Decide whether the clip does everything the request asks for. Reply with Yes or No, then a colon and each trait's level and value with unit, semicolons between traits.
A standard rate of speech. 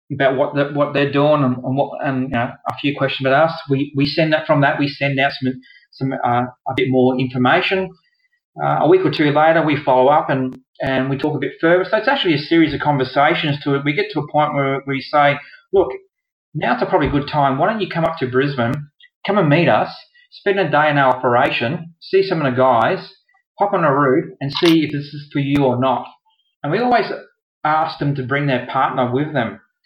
No: fast, 240 wpm